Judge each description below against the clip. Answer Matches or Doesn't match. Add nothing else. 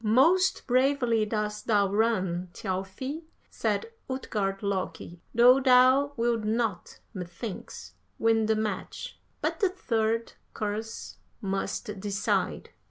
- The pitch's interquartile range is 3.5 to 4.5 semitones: Matches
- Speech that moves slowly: Matches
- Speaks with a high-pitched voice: Matches